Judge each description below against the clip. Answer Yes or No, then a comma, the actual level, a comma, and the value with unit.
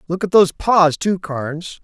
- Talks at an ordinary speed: Yes, average, 195 wpm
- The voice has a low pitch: No, medium, 175 Hz